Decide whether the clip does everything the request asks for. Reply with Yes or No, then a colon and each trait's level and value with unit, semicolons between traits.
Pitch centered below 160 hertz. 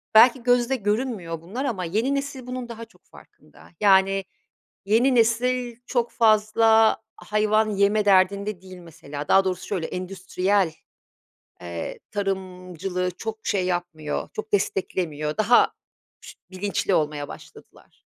No: high, 200 Hz